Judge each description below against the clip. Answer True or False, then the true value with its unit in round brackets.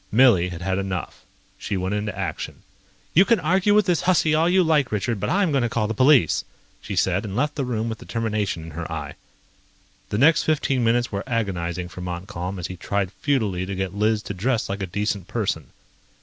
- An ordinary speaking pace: False (210 wpm)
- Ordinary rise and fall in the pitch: False (6.1 semitones)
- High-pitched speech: False (105 Hz)